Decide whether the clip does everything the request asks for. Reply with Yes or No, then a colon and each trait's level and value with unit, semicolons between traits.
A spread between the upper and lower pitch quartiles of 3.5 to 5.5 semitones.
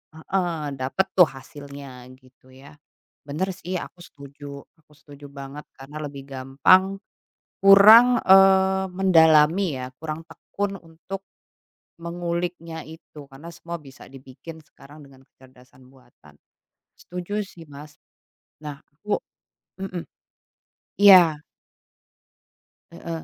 Yes: average, 4.5 semitones